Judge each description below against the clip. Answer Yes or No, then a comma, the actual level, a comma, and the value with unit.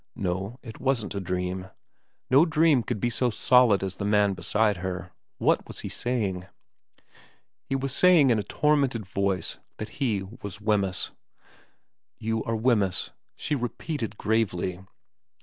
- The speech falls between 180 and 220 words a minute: No, average, 150 wpm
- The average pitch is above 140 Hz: No, low, 110 Hz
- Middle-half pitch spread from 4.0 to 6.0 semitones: Yes, average, 4.6 semitones